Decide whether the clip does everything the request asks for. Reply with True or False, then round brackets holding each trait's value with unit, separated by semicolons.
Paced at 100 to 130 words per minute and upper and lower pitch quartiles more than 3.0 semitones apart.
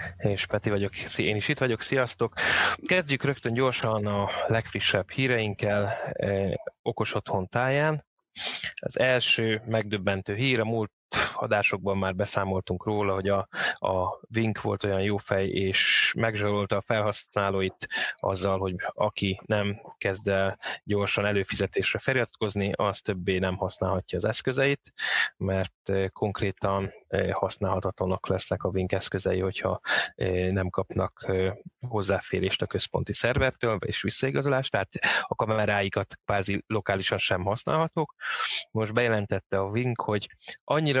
False (125 wpm; 2.7 semitones)